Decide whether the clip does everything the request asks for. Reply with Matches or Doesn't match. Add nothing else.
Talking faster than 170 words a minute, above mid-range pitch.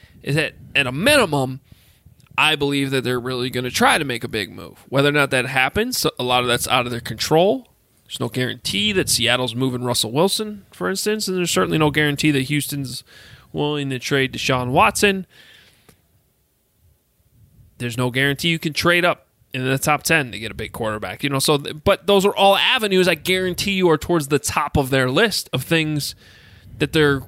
Doesn't match